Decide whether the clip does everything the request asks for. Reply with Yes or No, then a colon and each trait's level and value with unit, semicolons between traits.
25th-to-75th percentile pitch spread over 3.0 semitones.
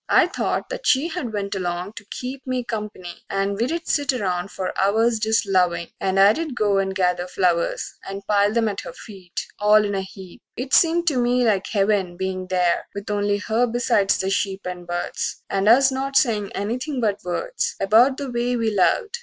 Yes: average, 4.3 semitones